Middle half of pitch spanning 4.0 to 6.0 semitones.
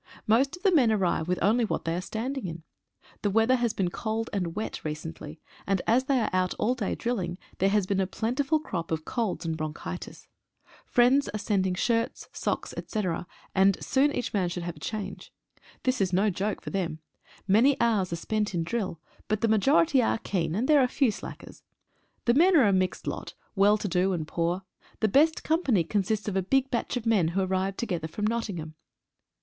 Yes: average, 4.8 semitones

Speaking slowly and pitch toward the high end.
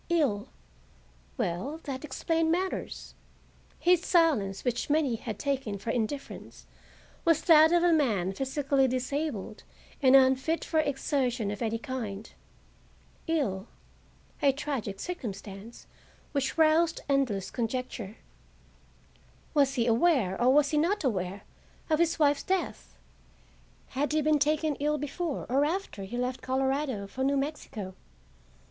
Yes: slow, 125 wpm; very high, 270 Hz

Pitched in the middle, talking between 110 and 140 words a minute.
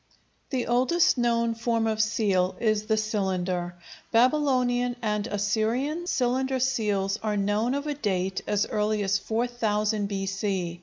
No: high, 220 Hz; slow, 135 wpm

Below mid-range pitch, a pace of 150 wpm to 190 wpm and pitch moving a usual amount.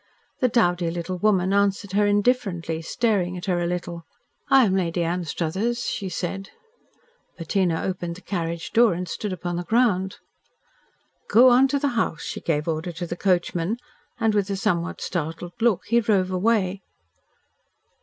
No: medium, 185 Hz; average, 160 wpm; average, 3.6 semitones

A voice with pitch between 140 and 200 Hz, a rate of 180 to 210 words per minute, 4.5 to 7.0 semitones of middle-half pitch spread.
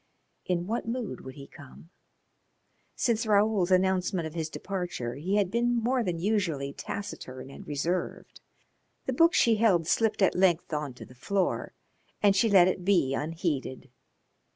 No: medium, 185 Hz; average, 155 wpm; average, 5.1 semitones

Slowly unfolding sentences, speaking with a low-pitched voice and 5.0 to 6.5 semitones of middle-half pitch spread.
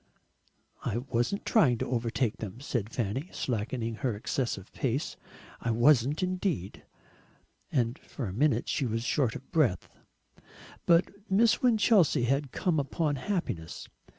Yes: slow, 130 wpm; low, 130 Hz; wide, 5.5 semitones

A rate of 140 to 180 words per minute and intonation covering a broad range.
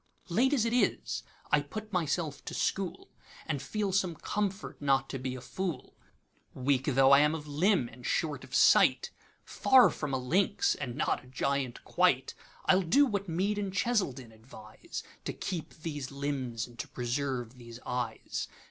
Yes: average, 155 wpm; wide, 6.8 semitones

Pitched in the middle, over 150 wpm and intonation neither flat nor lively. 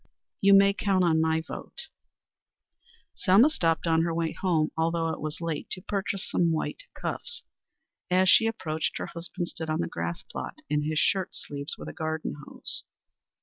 Yes: medium, 165 Hz; average, 175 wpm; average, 3.0 semitones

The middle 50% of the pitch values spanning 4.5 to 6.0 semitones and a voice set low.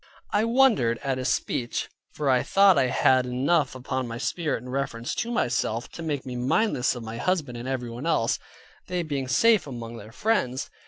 Yes: wide, 5.5 semitones; low, 130 Hz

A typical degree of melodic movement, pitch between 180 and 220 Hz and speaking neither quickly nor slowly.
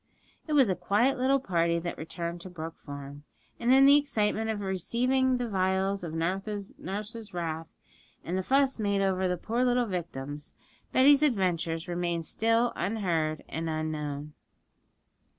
No: wide, 5.8 semitones; high, 190 Hz; average, 150 wpm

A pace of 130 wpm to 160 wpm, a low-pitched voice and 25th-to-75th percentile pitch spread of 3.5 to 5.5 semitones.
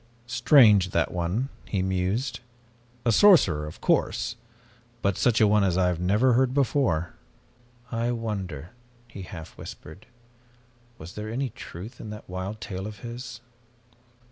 Yes: average, 140 wpm; low, 105 Hz; average, 4.5 semitones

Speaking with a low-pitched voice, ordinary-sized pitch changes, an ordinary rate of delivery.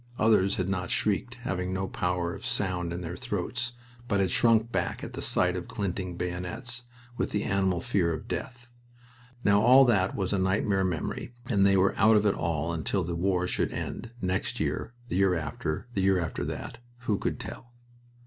Yes: very low, 95 Hz; average, 3.2 semitones; average, 195 wpm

